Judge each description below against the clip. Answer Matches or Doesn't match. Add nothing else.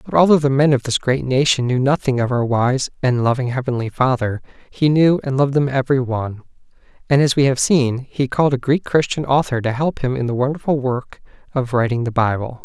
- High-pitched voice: Doesn't match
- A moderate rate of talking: Doesn't match